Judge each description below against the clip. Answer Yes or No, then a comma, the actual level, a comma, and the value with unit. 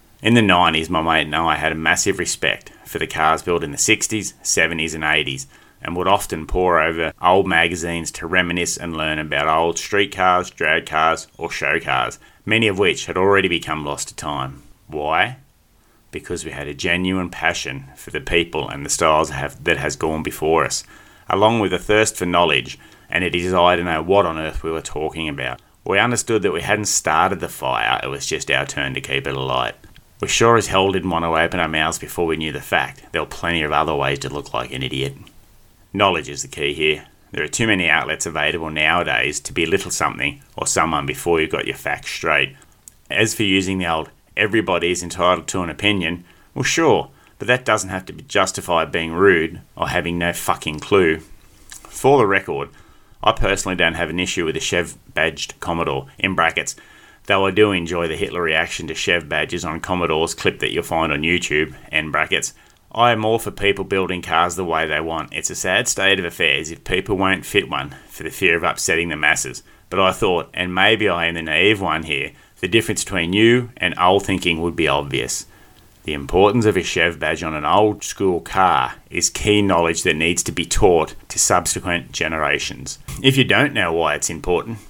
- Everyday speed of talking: No, fast, 210 wpm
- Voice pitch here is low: Yes, very low, 85 Hz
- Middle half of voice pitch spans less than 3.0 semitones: No, average, 3.5 semitones